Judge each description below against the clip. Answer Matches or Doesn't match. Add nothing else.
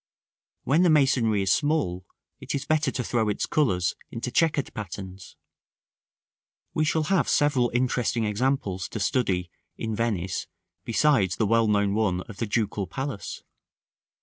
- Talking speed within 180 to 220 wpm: Doesn't match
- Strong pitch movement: Matches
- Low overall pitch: Matches